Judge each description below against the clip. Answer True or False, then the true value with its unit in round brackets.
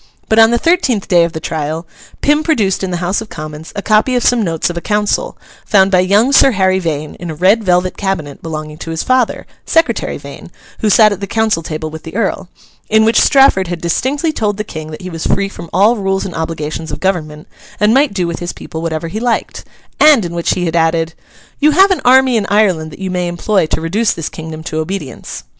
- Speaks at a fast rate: True (230 wpm)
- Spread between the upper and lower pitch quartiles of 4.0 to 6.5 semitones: True (5.2 semitones)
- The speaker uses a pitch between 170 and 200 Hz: True (190 Hz)